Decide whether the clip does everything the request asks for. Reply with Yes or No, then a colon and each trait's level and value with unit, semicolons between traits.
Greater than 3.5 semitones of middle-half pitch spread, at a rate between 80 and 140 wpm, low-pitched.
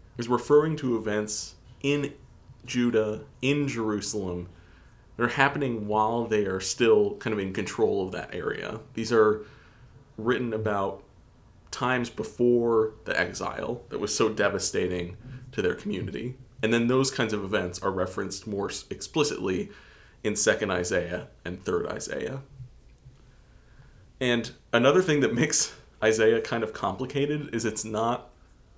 No: average, 3.0 semitones; slow, 135 wpm; low, 115 Hz